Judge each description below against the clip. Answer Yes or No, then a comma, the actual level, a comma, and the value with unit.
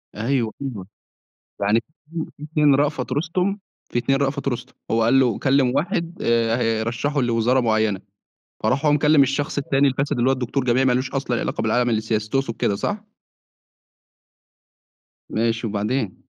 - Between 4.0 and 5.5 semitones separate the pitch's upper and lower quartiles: No, average, 3.6 semitones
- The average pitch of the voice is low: Yes, low, 130 Hz